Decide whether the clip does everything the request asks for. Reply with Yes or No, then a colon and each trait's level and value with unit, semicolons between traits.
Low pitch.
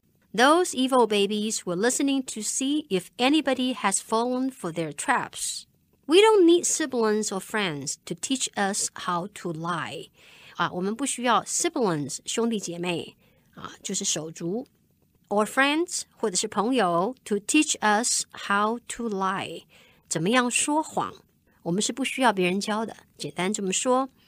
No: high, 215 Hz